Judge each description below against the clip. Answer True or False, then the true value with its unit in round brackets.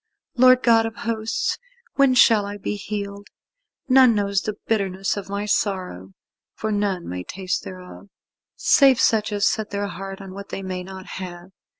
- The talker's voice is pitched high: True (200 Hz)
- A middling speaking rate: True (170 wpm)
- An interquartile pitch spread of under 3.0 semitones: True (2.5 semitones)